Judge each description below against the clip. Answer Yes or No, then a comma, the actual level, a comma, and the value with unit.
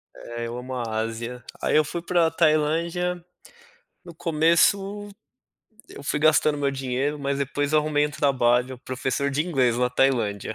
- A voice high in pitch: No, medium, 140 Hz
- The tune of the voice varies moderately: Yes, average, 4.0 semitones